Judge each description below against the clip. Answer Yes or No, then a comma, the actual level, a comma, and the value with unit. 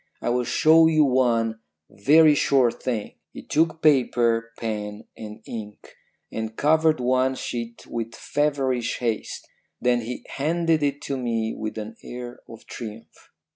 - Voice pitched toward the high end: No, low, 125 Hz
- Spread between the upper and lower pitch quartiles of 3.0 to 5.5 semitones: Yes, average, 4.2 semitones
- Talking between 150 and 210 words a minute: No, average, 140 wpm